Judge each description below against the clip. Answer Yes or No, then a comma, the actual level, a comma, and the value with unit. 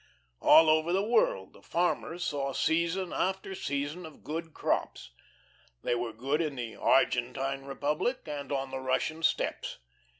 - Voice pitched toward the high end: No, medium, 150 Hz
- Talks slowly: No, average, 145 wpm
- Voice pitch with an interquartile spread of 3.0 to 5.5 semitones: Yes, average, 3.9 semitones